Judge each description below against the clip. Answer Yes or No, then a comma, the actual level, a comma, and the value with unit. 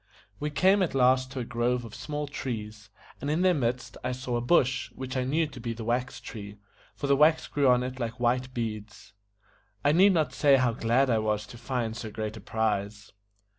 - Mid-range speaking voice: No, low, 125 Hz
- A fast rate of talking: Yes, fast, 215 wpm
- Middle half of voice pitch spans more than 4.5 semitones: No, average, 3.5 semitones